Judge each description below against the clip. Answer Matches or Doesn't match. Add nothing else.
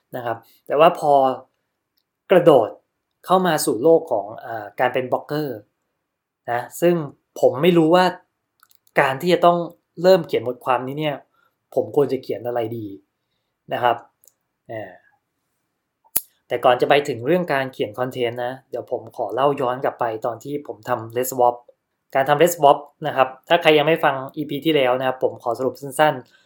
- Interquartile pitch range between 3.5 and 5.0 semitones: Matches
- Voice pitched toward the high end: Doesn't match